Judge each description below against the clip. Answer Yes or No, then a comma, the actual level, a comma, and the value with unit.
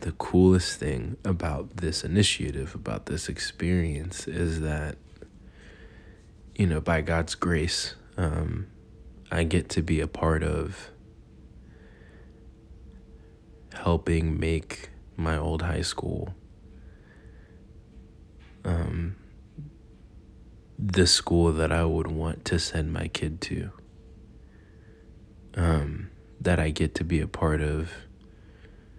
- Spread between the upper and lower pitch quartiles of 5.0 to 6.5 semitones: No, narrow, 2.6 semitones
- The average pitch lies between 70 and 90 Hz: Yes, very low, 80 Hz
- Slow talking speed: Yes, slow, 105 wpm